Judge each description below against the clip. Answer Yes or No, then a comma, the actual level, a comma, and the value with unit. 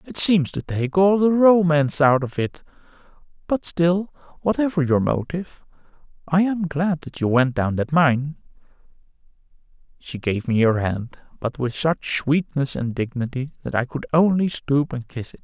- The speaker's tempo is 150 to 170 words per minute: Yes, average, 165 wpm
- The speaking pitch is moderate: Yes, medium, 150 Hz